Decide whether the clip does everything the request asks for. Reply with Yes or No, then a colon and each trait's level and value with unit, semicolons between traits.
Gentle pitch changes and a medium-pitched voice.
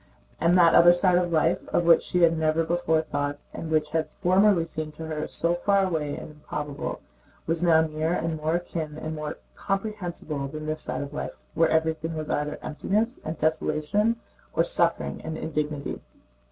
Yes: narrow, 2.2 semitones; medium, 160 Hz